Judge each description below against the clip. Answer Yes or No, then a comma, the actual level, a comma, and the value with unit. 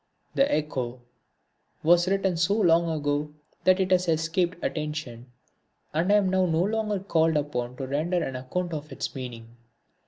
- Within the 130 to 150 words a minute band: No, average, 160 wpm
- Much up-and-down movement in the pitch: No, average, 4.1 semitones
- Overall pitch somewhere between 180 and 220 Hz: No, medium, 165 Hz